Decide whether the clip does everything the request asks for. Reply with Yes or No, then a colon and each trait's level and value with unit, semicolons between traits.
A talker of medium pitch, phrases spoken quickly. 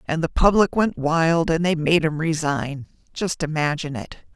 No: medium, 160 Hz; average, 165 wpm